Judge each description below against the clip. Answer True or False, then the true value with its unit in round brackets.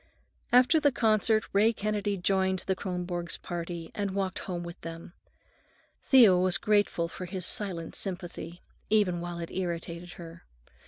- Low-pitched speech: False (185 Hz)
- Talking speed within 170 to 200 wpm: False (145 wpm)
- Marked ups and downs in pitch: False (2.9 semitones)